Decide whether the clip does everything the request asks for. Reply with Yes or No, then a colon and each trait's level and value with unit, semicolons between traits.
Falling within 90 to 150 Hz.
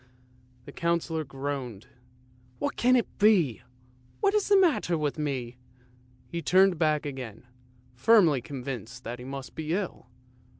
Yes: medium, 140 Hz